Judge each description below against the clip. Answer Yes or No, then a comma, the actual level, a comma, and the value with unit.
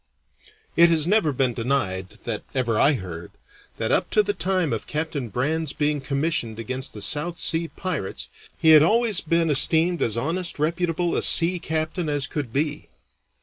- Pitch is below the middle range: No, medium, 155 Hz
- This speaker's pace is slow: No, average, 170 wpm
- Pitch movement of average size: Yes, average, 4.3 semitones